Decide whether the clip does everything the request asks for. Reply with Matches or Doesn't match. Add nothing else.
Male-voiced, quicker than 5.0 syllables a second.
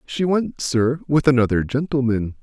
Doesn't match